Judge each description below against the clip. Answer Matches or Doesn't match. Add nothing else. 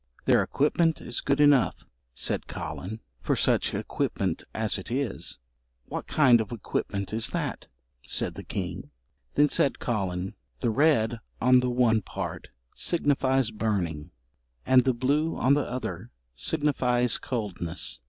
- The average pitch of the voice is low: Matches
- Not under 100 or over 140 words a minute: Matches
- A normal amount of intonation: Matches